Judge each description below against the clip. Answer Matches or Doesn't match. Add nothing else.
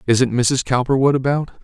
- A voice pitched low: Matches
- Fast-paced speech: Doesn't match